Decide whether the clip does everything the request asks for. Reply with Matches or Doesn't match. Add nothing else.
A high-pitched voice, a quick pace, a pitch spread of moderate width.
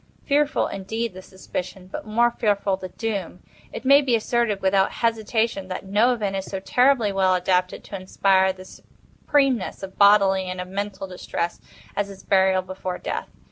Doesn't match